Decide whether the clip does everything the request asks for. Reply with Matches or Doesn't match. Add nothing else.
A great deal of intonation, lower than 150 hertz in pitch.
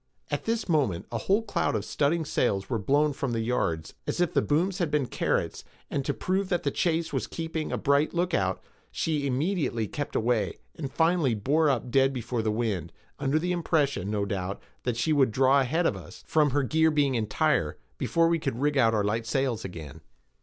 Matches